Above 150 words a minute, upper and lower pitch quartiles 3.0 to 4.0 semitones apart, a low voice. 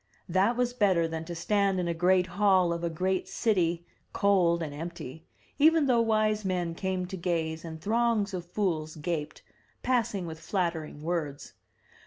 No: average, 165 wpm; average, 3.4 semitones; medium, 180 Hz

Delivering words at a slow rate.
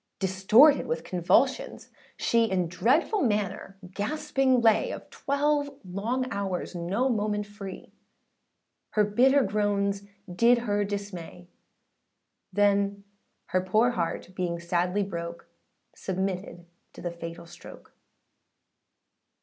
Yes: slow, 105 wpm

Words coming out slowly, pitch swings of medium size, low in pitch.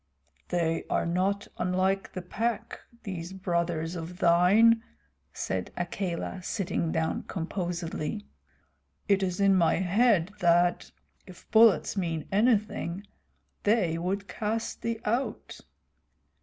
No: slow, 110 wpm; average, 3.1 semitones; medium, 185 Hz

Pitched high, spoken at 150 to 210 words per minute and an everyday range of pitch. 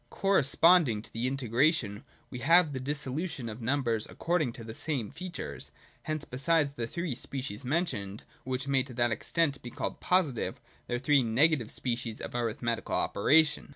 No: low, 130 Hz; average, 165 wpm; average, 4.7 semitones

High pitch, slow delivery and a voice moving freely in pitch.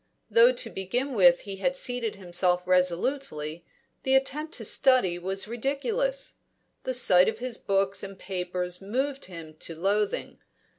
No: high, 200 Hz; average, 145 wpm; wide, 6.7 semitones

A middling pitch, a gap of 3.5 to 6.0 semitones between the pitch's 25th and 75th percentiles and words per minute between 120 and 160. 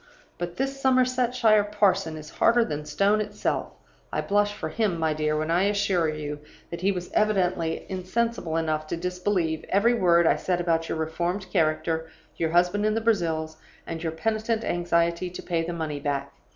No: medium, 175 Hz; average, 4.3 semitones; average, 180 wpm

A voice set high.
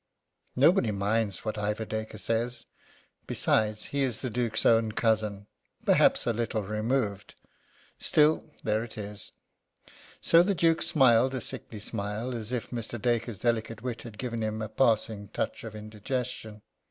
No: low, 115 Hz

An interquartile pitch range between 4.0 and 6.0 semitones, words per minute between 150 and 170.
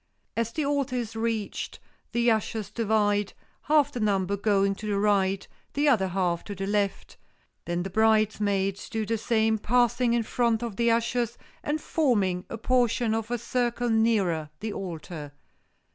No: average, 3.1 semitones; average, 160 wpm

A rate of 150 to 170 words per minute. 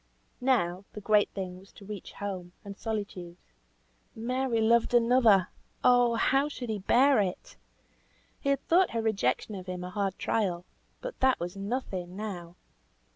Yes: average, 155 wpm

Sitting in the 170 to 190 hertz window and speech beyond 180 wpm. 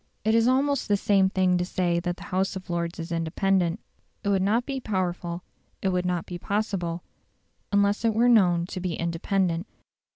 Yes: medium, 185 Hz; average, 190 wpm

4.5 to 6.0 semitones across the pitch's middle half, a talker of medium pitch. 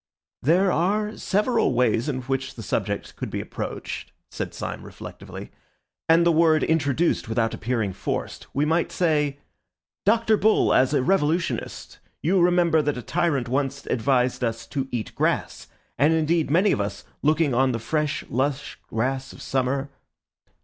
Yes: average, 4.8 semitones; medium, 145 Hz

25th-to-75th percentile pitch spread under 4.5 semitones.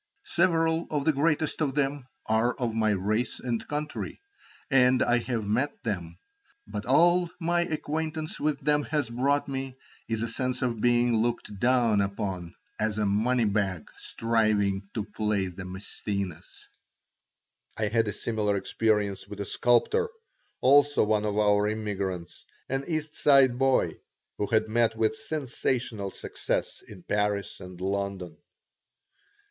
No: average, 5.1 semitones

